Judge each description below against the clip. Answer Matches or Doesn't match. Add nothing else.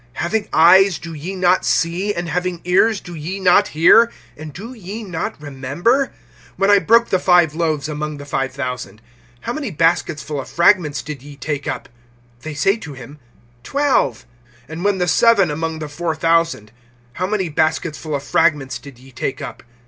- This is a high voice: Doesn't match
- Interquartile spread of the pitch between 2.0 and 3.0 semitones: Doesn't match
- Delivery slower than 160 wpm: Doesn't match